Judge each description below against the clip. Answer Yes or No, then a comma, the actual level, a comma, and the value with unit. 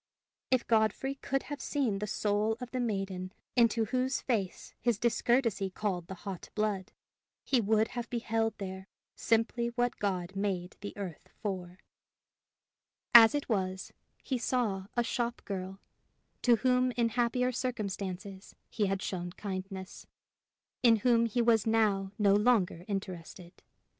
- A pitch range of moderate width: Yes, average, 3.7 semitones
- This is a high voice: Yes, high, 215 Hz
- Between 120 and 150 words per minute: Yes, average, 140 wpm